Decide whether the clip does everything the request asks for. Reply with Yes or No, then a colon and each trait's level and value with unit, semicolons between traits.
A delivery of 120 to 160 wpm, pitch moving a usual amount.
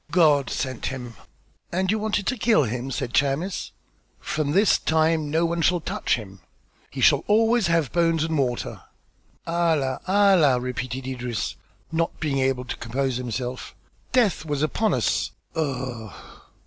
Yes: average, 150 wpm; average, 5.0 semitones